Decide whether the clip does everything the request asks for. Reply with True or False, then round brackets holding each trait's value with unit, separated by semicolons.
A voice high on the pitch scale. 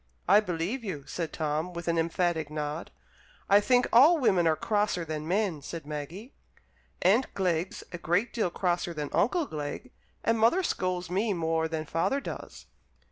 False (175 Hz)